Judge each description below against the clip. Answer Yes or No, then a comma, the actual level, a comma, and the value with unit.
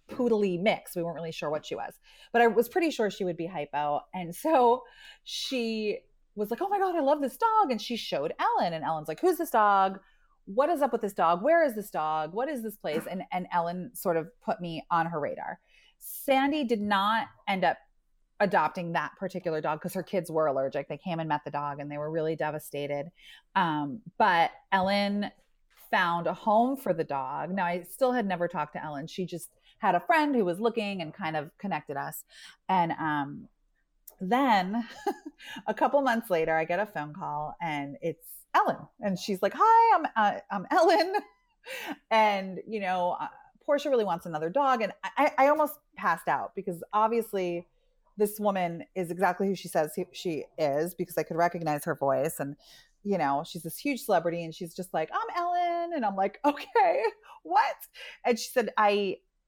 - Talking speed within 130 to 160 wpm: No, average, 200 wpm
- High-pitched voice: Yes, high, 195 Hz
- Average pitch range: No, wide, 7.3 semitones